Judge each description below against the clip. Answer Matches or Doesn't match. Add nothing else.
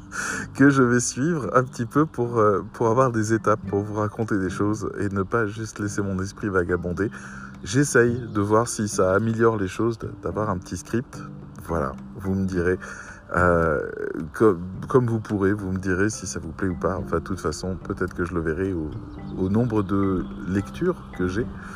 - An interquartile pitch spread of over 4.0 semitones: Doesn't match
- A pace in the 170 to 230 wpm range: Matches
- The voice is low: Matches